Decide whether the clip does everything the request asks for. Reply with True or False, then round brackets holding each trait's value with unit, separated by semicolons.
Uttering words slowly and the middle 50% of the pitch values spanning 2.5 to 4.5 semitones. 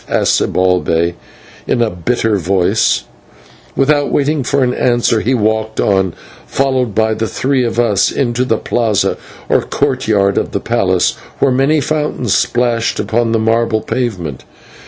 False (150 wpm; 3.6 semitones)